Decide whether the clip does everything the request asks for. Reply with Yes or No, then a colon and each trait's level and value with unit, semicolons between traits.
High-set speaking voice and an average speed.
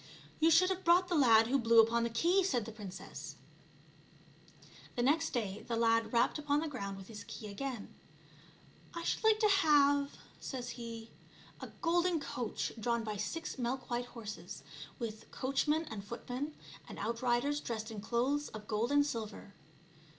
Yes: high, 245 Hz; average, 180 wpm